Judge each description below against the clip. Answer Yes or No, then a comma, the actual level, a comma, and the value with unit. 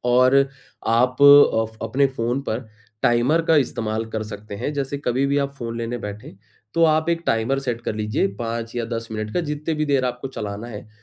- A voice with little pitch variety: No, average, 3.7 semitones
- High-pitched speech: No, low, 120 Hz